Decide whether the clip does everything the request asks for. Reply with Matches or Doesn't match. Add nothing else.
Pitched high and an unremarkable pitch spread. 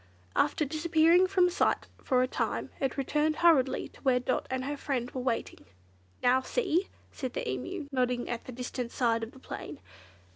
Matches